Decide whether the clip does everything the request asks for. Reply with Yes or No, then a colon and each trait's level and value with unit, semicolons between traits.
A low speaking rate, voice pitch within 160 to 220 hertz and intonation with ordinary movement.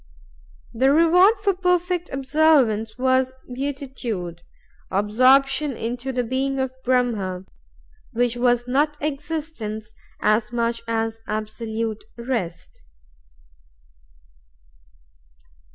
No: slow, 90 wpm; very high, 250 Hz; average, 3.7 semitones